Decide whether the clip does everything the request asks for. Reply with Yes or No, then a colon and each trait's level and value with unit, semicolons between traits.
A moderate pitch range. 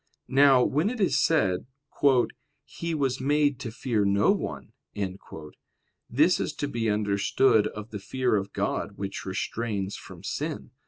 No: wide, 5.8 semitones